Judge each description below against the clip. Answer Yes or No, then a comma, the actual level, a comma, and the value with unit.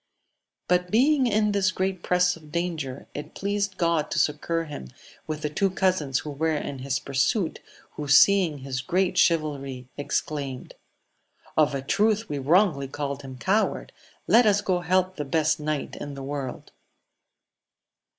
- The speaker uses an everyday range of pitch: Yes, average, 5.0 semitones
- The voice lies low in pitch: No, medium, 155 Hz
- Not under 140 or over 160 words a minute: Yes, average, 155 wpm